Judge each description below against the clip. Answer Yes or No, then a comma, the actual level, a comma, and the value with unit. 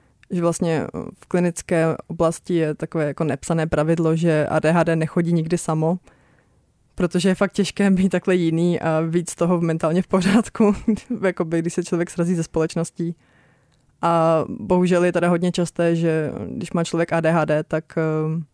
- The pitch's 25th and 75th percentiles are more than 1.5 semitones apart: Yes, narrow, 1.9 semitones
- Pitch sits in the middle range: Yes, medium, 170 Hz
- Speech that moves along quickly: No, average, 155 wpm